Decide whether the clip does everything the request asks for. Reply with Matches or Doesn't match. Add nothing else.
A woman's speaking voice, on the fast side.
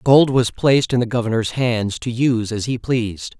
Doesn't match